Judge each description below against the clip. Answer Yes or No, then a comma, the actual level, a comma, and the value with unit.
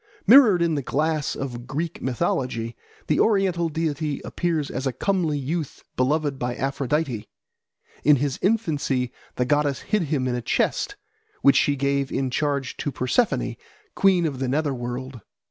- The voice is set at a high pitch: No, medium, 145 Hz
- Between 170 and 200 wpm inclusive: No, average, 155 wpm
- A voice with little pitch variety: No, average, 3.8 semitones